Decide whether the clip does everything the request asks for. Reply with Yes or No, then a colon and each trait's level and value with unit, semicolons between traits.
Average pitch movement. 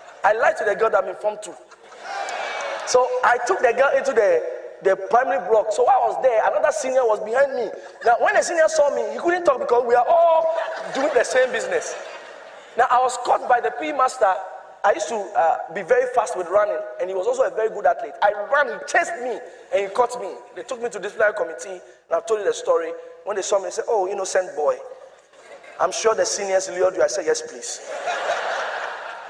No: wide, 9.0 semitones